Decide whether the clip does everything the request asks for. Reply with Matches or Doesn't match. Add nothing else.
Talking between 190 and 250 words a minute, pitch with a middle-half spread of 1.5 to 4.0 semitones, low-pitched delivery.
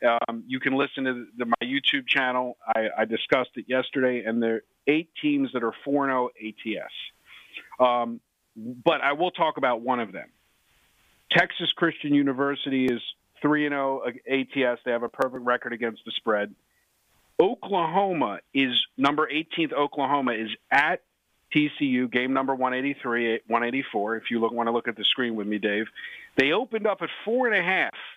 Doesn't match